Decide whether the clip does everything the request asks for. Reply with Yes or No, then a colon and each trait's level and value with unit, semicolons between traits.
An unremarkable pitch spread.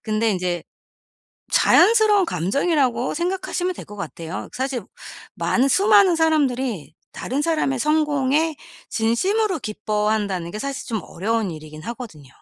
No: wide, 7.4 semitones